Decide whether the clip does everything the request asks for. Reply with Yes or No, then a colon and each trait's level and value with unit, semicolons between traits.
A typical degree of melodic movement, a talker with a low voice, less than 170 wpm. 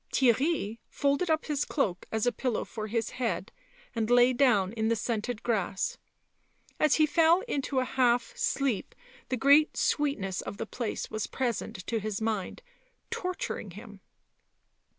No: average, 4.6 semitones; high, 245 Hz; average, 150 wpm